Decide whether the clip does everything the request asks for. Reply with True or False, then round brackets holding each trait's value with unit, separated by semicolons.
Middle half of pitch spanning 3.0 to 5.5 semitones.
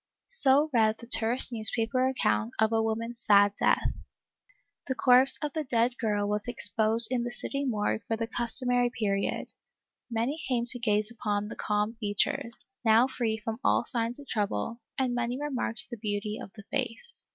False (2.5 semitones)